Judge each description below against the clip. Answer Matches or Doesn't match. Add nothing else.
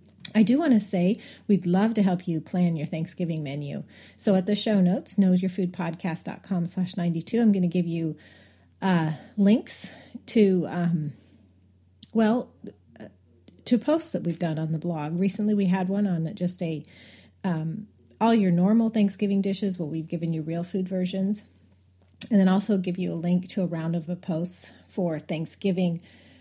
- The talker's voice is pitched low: Doesn't match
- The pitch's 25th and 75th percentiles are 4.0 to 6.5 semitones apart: Doesn't match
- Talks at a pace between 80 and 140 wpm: Doesn't match